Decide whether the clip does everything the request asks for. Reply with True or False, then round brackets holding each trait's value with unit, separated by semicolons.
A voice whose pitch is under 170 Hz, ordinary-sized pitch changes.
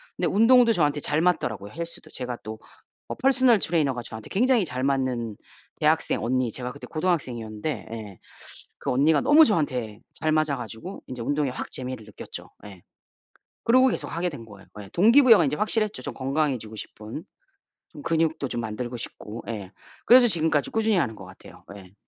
False (140 Hz; 7.5 semitones)